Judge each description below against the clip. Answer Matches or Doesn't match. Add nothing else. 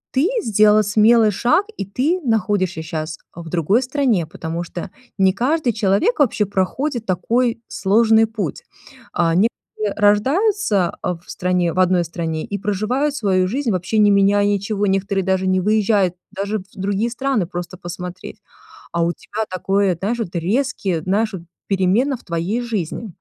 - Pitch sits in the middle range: Doesn't match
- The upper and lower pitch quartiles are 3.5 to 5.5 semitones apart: Matches